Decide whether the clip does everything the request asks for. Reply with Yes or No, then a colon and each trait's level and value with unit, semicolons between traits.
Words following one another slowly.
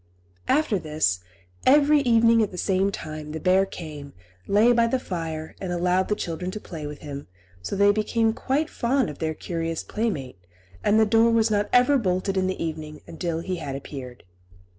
No: average, 185 wpm